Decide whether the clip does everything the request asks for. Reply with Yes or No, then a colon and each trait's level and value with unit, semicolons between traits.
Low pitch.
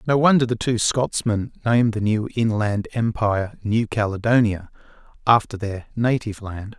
Yes: low, 110 Hz